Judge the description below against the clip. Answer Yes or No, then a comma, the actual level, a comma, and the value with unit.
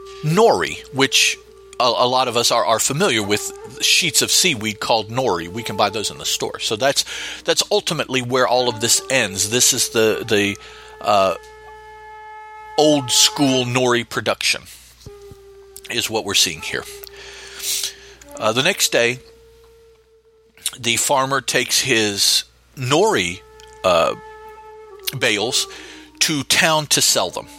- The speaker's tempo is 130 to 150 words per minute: Yes, slow, 135 wpm